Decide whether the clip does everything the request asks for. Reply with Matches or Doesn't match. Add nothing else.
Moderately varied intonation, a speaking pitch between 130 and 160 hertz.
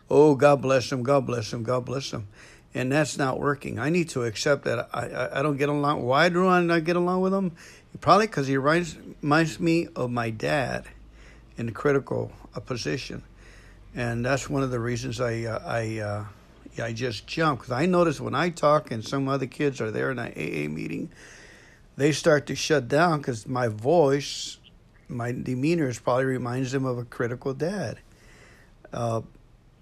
Matches